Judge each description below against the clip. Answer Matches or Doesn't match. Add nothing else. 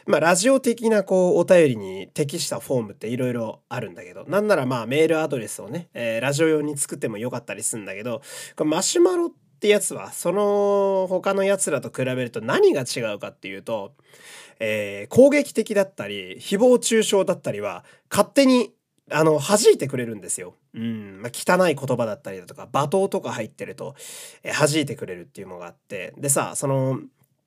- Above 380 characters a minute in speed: Matches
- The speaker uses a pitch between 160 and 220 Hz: Matches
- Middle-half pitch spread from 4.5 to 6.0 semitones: Doesn't match